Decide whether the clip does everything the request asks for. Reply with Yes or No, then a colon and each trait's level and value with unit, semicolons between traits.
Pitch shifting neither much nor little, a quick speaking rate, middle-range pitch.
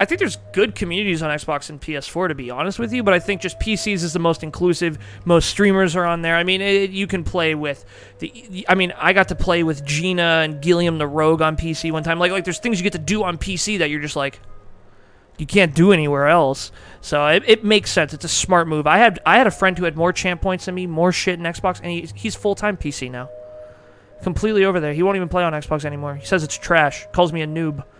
Yes: average, 4.0 semitones; fast, 260 wpm; medium, 170 Hz